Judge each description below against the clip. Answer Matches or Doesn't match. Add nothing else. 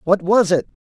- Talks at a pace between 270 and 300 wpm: Doesn't match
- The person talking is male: Matches